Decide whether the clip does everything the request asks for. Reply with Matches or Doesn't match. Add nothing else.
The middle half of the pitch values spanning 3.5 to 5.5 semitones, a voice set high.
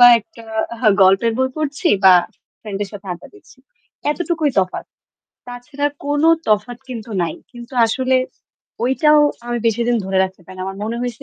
Matches